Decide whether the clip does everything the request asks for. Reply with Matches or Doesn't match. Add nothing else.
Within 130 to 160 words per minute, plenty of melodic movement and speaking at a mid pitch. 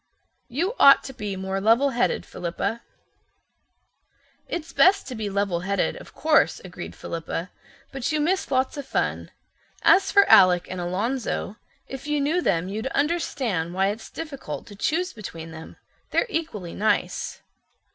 Doesn't match